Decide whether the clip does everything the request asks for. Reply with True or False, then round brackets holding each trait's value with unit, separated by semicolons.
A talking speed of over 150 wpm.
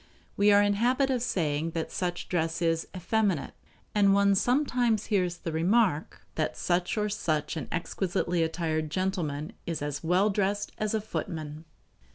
True (165 wpm)